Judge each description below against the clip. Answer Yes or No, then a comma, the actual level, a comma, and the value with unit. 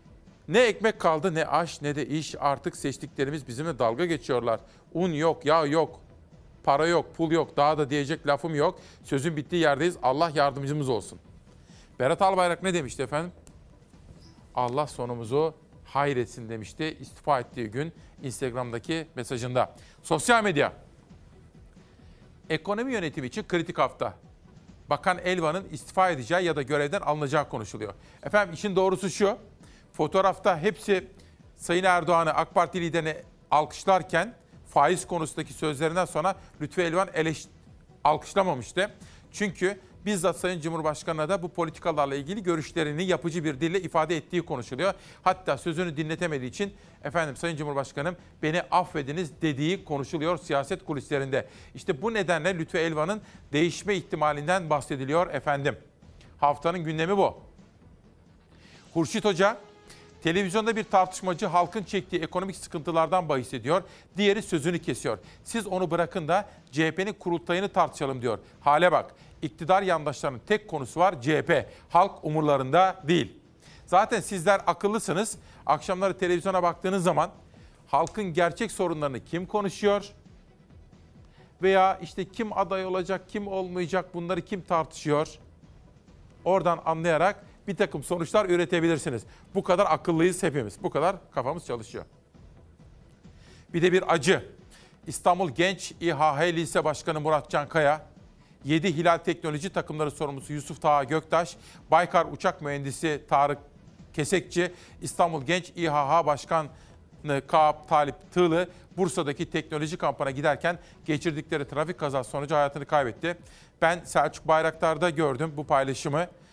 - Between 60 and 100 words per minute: No, average, 125 wpm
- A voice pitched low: No, medium, 165 Hz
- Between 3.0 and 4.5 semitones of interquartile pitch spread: Yes, average, 3.6 semitones